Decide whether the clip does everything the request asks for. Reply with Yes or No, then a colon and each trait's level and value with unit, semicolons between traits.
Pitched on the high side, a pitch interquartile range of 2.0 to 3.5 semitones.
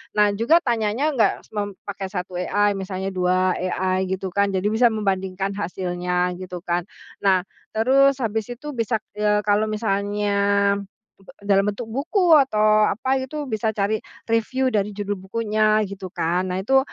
Yes: high, 205 Hz; average, 2.8 semitones